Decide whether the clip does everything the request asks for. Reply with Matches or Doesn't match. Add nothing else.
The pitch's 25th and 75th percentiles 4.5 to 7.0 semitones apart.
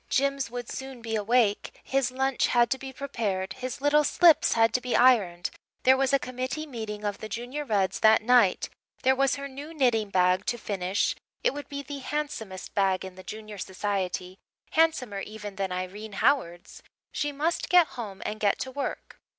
Matches